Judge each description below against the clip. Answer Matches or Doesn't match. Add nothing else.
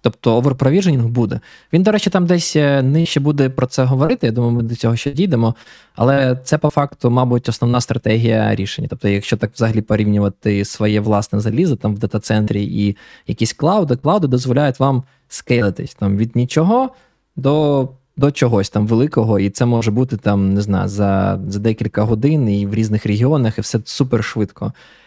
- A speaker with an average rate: Doesn't match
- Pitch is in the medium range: Doesn't match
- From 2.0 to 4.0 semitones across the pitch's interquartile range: Doesn't match